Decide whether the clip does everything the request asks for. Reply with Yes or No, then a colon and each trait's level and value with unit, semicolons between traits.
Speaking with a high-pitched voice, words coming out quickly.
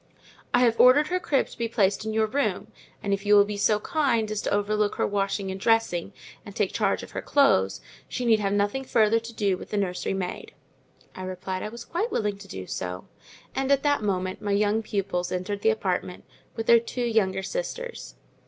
Yes: high, 210 Hz; fast, 215 wpm